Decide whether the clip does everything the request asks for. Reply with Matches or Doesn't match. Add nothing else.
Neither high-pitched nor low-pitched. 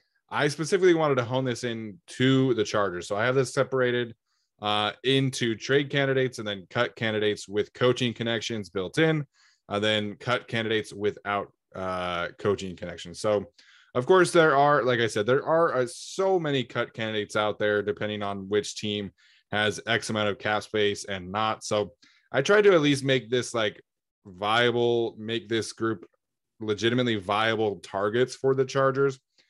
Doesn't match